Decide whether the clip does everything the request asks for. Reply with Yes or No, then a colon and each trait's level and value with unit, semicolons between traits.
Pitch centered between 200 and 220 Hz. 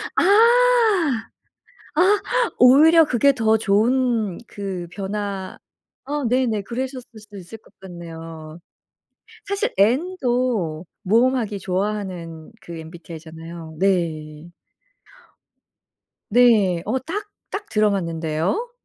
Yes: high, 205 Hz